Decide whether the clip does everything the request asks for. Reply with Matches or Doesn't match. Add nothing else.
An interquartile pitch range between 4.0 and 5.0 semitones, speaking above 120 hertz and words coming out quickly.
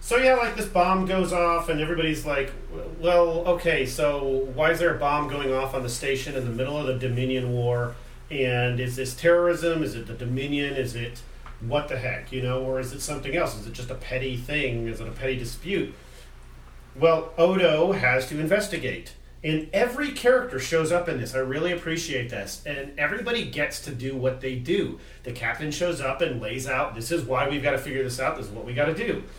Matches